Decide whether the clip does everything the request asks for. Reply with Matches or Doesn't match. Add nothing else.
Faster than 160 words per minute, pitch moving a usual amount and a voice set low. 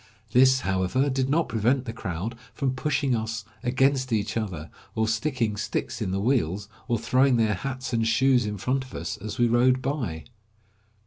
Matches